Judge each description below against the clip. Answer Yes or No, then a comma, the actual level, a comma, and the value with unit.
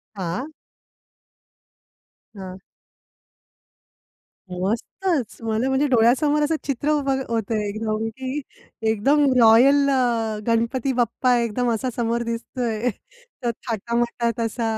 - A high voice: Yes, high, 235 Hz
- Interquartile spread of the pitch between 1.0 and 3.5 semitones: Yes, average, 3.0 semitones